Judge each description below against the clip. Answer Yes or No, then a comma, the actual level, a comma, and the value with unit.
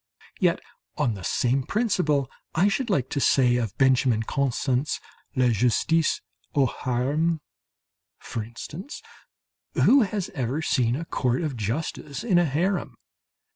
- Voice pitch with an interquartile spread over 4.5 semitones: Yes, average, 5.2 semitones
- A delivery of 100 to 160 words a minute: Yes, slow, 135 wpm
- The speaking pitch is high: No, medium, 140 Hz